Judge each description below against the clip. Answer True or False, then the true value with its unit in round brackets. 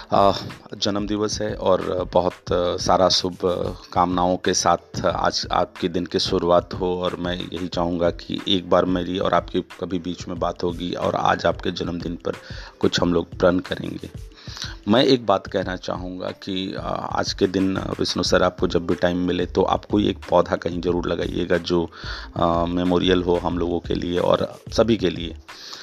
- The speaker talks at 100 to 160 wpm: False (170 wpm)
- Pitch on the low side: True (90 Hz)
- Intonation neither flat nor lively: False (1.1 semitones)